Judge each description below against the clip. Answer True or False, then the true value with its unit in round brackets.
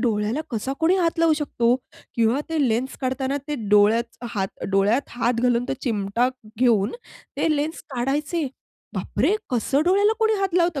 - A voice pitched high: True (255 Hz)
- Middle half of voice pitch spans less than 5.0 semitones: False (5.3 semitones)